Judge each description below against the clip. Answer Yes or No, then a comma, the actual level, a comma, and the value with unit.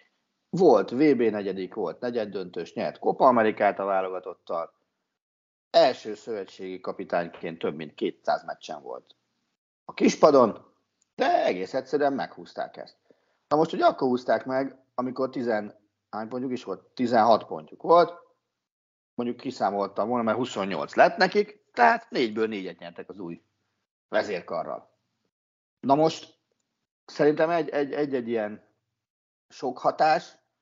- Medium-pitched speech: No, low, 120 Hz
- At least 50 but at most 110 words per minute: No, average, 120 wpm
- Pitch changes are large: Yes, wide, 6.6 semitones